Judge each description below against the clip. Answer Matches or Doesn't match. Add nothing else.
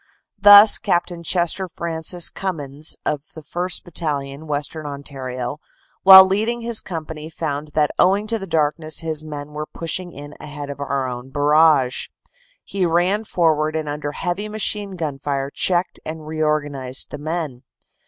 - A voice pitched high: Doesn't match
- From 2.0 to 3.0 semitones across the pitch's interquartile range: Doesn't match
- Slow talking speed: Doesn't match